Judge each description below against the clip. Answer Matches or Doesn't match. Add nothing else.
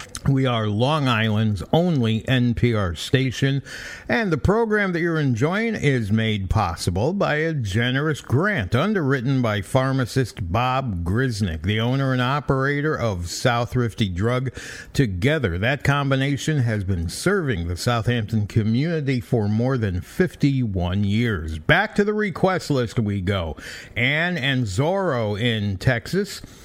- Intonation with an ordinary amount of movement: Matches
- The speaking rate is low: Matches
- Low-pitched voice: Matches